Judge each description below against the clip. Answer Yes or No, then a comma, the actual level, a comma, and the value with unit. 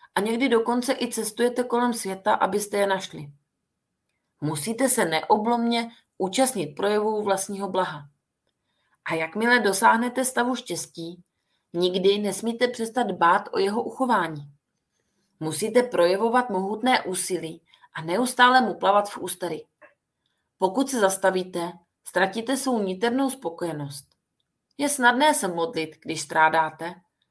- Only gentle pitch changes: No, wide, 5.8 semitones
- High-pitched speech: Yes, high, 195 Hz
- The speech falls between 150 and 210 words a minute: No, slow, 115 wpm